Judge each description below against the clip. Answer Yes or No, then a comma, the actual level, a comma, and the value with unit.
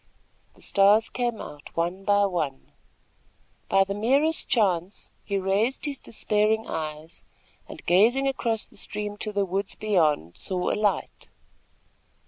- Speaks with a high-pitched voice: Yes, high, 200 Hz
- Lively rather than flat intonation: No, average, 3.6 semitones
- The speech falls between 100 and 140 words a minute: Yes, slow, 135 wpm